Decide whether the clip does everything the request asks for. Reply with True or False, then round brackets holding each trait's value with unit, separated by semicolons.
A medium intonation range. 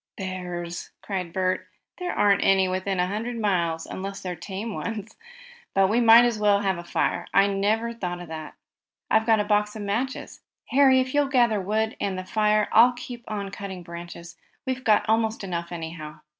True (3.5 semitones)